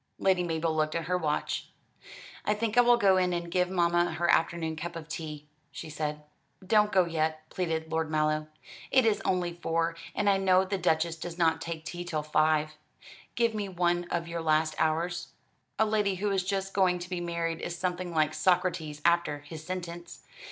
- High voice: No, medium, 170 Hz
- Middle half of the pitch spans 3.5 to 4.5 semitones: No, narrow, 2.5 semitones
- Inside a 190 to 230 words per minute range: Yes, average, 195 wpm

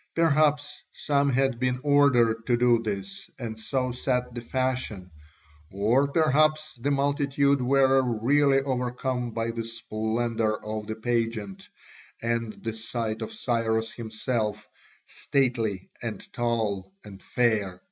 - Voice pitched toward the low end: Yes, low, 120 Hz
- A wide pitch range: No, average, 3.4 semitones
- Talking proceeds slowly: Yes, slow, 125 wpm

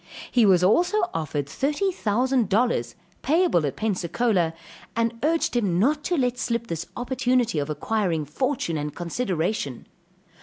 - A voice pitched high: Yes, high, 220 Hz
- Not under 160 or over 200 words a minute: No, average, 140 wpm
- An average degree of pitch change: No, wide, 7.3 semitones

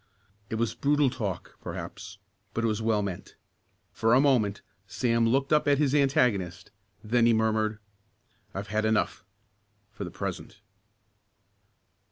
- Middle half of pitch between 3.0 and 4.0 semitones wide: Yes, average, 3.6 semitones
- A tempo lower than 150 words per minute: Yes, average, 140 wpm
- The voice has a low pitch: Yes, low, 115 Hz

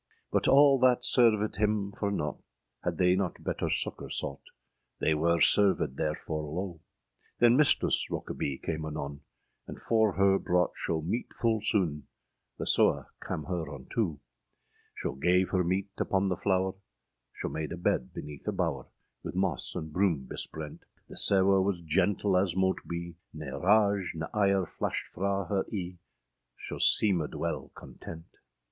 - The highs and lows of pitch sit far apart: No, average, 4.0 semitones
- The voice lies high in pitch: No, very low, 90 Hz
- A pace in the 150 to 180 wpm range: Yes, average, 155 wpm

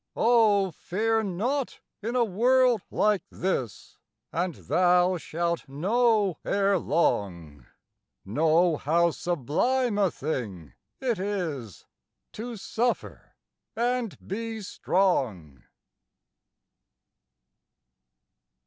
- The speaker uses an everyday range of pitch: No, wide, 6.2 semitones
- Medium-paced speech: No, slow, 85 wpm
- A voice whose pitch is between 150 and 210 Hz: Yes, medium, 185 Hz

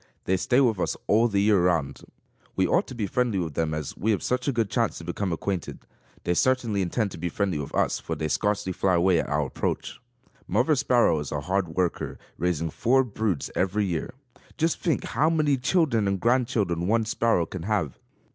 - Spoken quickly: Yes, fast, 210 wpm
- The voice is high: No, low, 100 Hz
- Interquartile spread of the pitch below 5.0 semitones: No, wide, 5.5 semitones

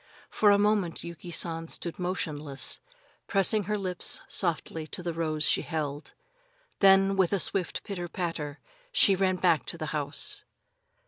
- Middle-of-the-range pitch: Yes, medium, 175 Hz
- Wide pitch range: No, average, 3.2 semitones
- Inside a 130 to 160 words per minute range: Yes, average, 150 wpm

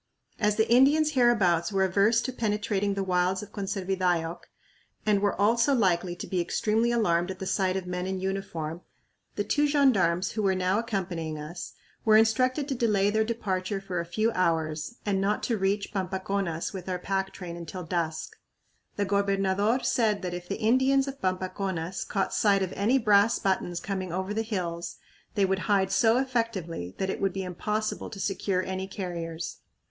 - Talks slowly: No, average, 180 wpm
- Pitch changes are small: No, average, 3.1 semitones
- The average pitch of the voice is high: Yes, high, 195 Hz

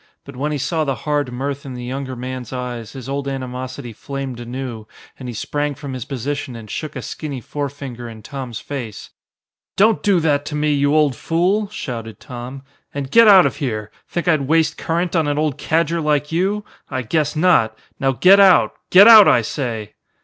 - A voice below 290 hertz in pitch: Yes, medium, 140 Hz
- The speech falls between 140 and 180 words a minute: No, average, 195 wpm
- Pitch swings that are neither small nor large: Yes, average, 3.7 semitones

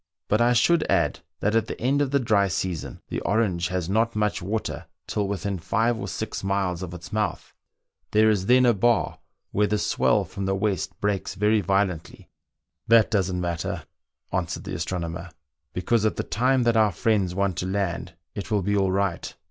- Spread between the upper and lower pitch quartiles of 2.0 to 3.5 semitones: Yes, average, 3.1 semitones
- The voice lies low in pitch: Yes, low, 100 Hz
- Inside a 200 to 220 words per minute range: Yes, fast, 205 wpm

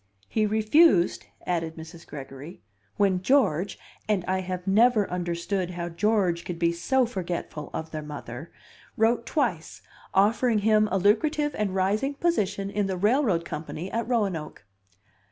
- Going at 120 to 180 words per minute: Yes, average, 140 wpm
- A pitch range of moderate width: Yes, average, 4.3 semitones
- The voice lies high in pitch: Yes, high, 195 Hz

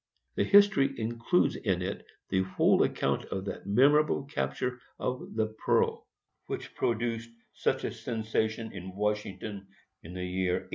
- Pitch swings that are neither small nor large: Yes, average, 4.5 semitones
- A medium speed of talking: Yes, average, 145 wpm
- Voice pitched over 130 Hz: No, low, 110 Hz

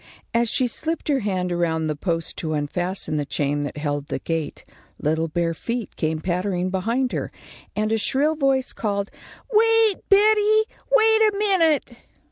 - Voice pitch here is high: Yes, high, 200 Hz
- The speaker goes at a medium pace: Yes, average, 160 wpm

